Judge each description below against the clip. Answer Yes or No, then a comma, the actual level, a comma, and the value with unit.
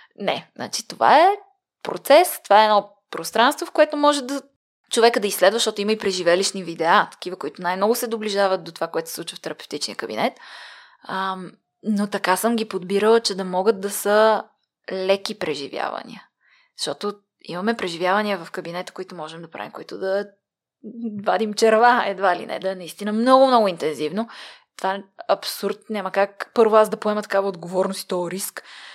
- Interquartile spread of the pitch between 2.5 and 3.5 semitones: Yes, average, 3.1 semitones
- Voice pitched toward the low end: No, high, 205 Hz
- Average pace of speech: No, fast, 170 wpm